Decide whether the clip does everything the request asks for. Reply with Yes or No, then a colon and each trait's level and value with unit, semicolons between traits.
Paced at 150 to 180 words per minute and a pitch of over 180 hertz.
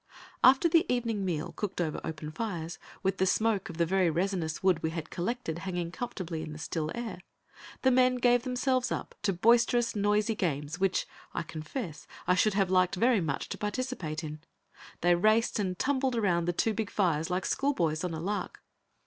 No: average, 190 wpm; high, 190 Hz